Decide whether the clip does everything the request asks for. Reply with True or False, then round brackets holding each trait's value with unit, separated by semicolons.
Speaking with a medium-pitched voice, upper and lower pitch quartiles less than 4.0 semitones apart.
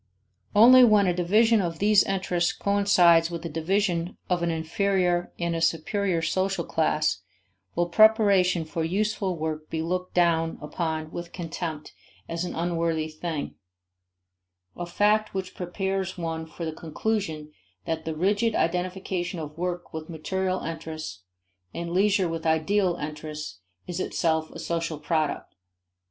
True (170 Hz; 2.9 semitones)